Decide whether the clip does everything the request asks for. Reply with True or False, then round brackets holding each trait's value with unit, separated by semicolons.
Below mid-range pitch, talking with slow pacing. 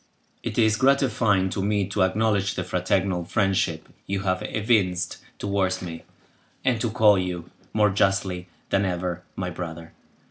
False (95 Hz; 145 wpm)